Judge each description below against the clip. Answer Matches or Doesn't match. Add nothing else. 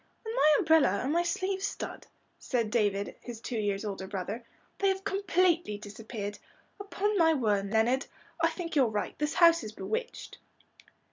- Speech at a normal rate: Matches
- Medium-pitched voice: Doesn't match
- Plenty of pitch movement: Matches